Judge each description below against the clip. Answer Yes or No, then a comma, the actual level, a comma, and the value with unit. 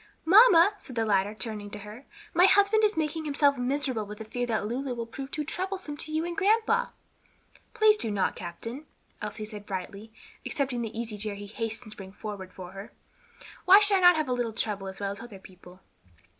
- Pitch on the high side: Yes, high, 235 Hz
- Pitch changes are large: Yes, wide, 7.2 semitones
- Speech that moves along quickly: Yes, fast, 210 wpm